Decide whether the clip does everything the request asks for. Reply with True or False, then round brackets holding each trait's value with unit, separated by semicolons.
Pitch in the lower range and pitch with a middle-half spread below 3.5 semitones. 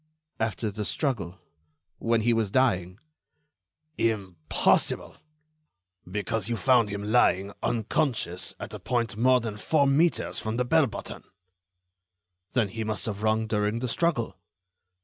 True (110 Hz; 3.0 semitones)